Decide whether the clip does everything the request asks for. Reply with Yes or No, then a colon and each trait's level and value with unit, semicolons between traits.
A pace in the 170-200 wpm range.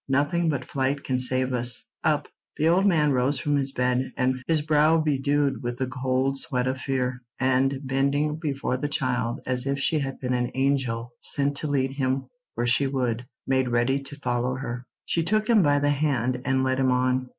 Yes: average, 195 wpm